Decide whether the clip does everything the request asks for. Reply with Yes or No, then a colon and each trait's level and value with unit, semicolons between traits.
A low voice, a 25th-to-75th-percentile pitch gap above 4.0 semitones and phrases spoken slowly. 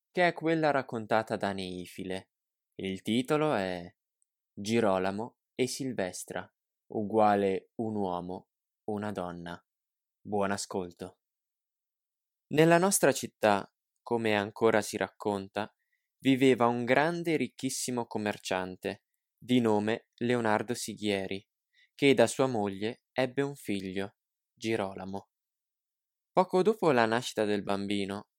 Yes: low, 110 Hz; average, 4.5 semitones; slow, 105 wpm